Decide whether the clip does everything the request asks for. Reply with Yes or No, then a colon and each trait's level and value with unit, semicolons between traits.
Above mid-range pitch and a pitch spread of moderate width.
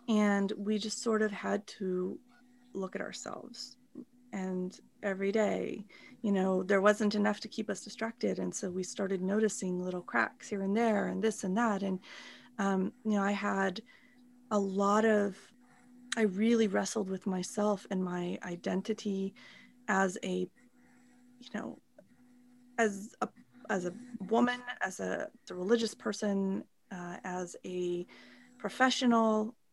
Yes: high, 210 Hz; average, 3.7 semitones